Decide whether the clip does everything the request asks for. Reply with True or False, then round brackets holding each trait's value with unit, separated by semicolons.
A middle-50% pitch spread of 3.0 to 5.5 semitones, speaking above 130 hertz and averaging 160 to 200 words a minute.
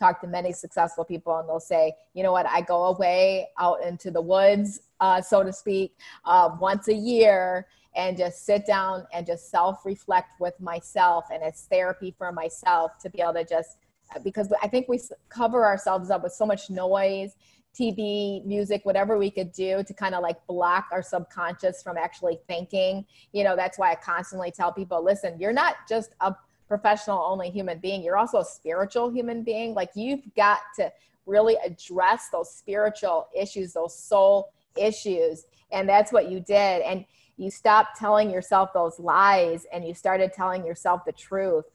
False (2.6 semitones; 190 Hz; 185 wpm)